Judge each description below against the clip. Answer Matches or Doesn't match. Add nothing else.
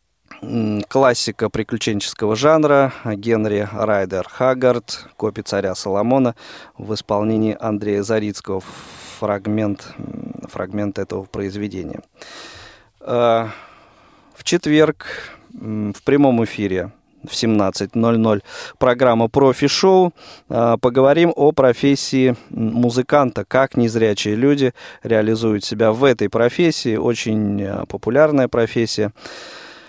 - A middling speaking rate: Doesn't match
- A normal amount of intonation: Matches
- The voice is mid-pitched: Doesn't match